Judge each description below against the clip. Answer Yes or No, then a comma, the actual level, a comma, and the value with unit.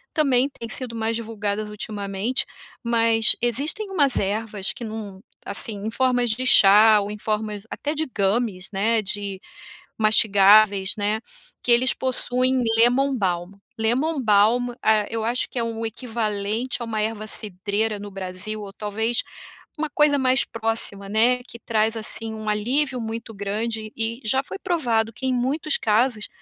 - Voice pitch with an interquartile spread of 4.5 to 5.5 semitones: No, average, 2.8 semitones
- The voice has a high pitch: Yes, high, 225 Hz